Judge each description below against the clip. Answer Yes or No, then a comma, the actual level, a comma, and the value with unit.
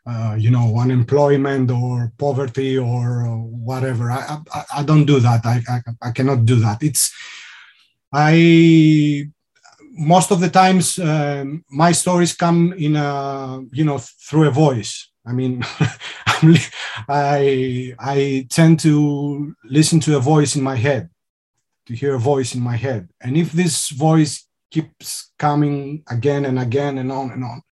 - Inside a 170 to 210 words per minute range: No, average, 150 wpm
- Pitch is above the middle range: No, medium, 140 Hz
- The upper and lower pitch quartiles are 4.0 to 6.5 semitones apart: No, average, 3.4 semitones